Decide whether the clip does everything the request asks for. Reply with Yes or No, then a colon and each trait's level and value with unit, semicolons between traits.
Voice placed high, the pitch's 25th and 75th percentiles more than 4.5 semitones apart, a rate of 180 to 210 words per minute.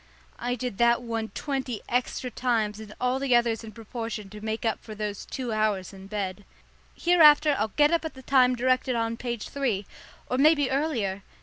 No: high, 235 Hz; average, 3.4 semitones; average, 190 wpm